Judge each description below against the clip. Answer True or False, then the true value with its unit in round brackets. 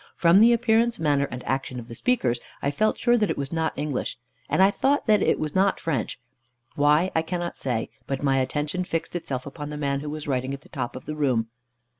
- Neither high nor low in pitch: True (150 Hz)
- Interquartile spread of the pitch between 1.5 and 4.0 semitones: False (5.2 semitones)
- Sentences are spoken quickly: True (230 wpm)